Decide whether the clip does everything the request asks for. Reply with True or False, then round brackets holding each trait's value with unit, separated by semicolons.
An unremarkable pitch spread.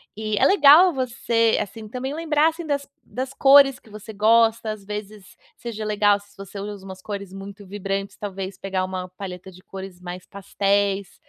True (3.2 semitones)